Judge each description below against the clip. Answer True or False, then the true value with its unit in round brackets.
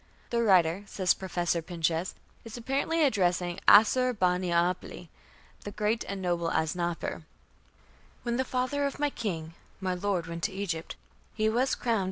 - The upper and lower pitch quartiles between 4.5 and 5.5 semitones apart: True (5.2 semitones)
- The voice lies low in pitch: False (190 Hz)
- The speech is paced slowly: False (150 wpm)